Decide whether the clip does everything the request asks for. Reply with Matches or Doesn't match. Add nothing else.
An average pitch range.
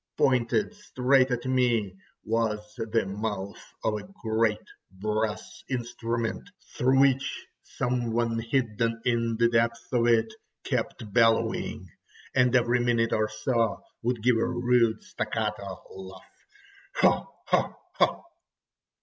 Doesn't match